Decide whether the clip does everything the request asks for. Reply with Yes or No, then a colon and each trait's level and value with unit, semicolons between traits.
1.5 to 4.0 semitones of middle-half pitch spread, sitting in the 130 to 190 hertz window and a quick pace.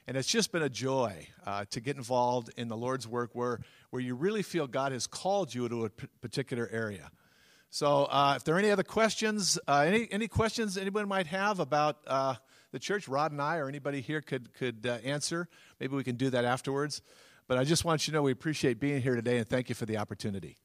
No: average, 5.1 semitones; low, 135 Hz; fast, 230 wpm